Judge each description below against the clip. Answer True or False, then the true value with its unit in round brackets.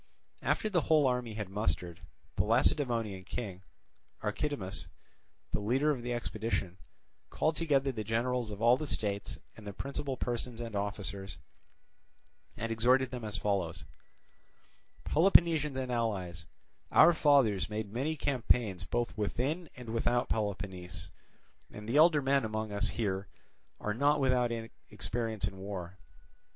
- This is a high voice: False (115 Hz)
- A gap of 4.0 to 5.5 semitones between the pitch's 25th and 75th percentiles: True (4.6 semitones)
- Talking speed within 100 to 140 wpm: True (135 wpm)